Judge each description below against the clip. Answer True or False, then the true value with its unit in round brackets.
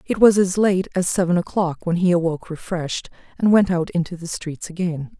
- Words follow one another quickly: True (210 wpm)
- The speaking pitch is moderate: True (175 Hz)